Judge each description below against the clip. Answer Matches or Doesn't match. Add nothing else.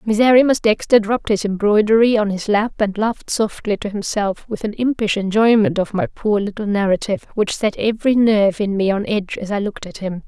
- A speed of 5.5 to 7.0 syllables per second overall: Matches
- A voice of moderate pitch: Doesn't match